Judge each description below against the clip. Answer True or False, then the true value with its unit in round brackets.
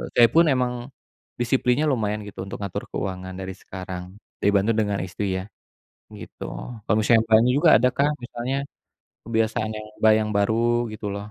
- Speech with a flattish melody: False (3.2 semitones)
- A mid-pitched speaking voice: False (110 Hz)